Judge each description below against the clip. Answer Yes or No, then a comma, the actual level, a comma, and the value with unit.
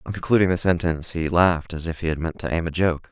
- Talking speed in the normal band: No, fast, 290 wpm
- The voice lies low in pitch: Yes, very low, 85 Hz